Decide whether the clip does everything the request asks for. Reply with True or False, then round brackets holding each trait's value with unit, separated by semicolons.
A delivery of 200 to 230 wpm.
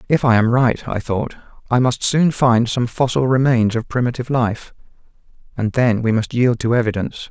False (190 wpm)